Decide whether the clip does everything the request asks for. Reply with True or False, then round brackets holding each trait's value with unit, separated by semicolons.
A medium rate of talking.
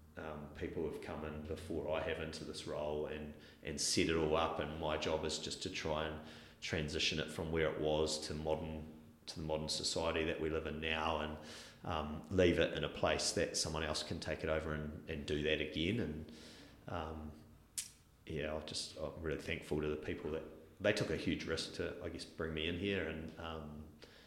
False (220 wpm)